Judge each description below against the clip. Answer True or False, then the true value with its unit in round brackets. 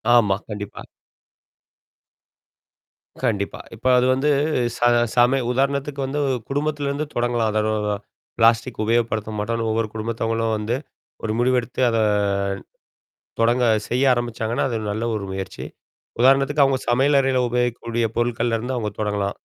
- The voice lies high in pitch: False (120 Hz)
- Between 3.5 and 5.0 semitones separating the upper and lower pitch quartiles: False (2.8 semitones)